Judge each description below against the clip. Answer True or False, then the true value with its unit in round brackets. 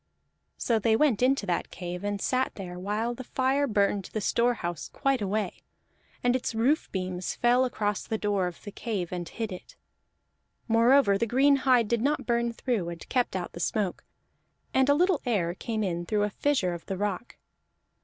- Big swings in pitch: False (4.8 semitones)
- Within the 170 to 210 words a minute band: True (185 wpm)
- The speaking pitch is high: True (220 Hz)